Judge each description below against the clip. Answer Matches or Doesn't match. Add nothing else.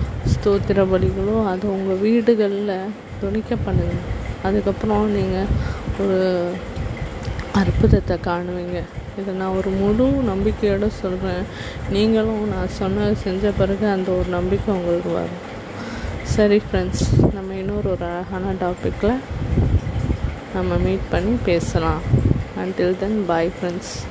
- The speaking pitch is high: Matches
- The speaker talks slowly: Doesn't match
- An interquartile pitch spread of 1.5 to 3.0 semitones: Matches